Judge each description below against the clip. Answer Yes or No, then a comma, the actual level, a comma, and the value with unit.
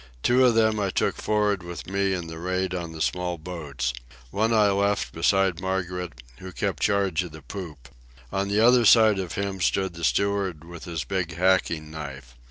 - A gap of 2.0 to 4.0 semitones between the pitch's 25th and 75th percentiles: Yes, average, 3.3 semitones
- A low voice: Yes, very low, 95 Hz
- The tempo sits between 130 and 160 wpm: No, average, 190 wpm